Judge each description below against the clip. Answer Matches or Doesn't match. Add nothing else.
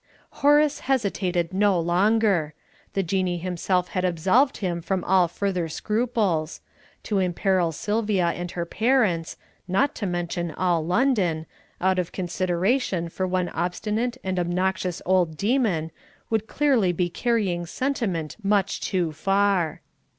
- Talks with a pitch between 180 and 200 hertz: Matches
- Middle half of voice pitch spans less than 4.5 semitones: Matches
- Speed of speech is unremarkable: Doesn't match